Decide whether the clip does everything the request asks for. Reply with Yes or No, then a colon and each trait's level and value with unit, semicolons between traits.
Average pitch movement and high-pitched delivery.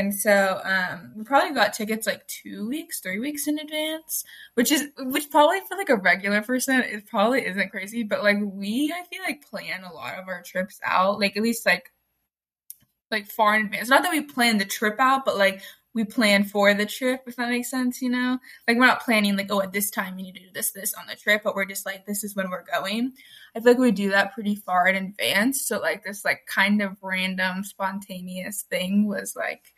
Yes: average, 4.5 semitones; high, 210 Hz